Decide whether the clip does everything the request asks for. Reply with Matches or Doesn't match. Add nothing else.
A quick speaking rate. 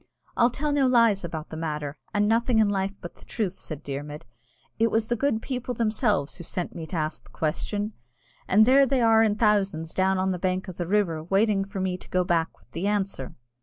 Matches